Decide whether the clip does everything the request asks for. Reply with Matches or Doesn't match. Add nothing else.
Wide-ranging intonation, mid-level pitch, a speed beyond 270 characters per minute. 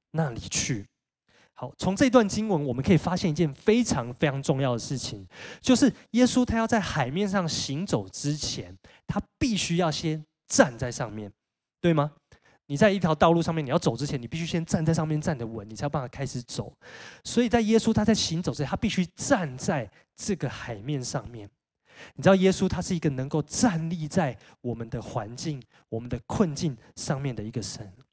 Matches